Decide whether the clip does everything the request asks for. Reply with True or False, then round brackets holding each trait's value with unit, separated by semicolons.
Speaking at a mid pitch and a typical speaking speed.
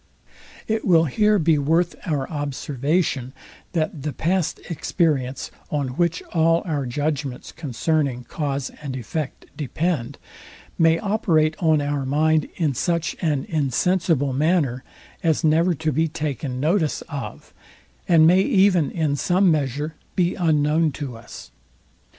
False (155 Hz; 130 wpm)